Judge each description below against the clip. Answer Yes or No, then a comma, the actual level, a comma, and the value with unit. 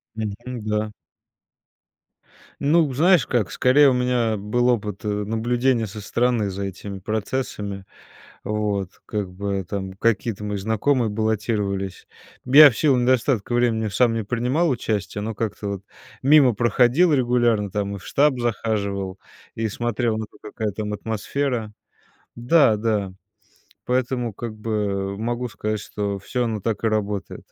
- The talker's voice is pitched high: No, low, 110 Hz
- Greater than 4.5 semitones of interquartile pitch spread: No, average, 3.1 semitones